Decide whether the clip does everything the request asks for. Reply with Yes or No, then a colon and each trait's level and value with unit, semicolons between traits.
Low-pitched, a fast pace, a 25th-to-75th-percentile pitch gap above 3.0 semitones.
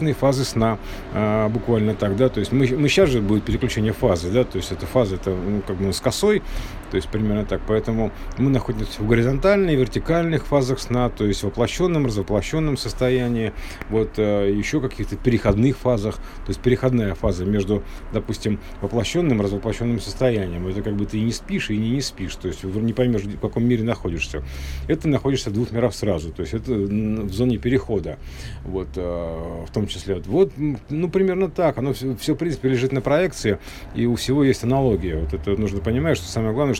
Yes: low, 110 Hz; fast, 195 wpm; average, 4.6 semitones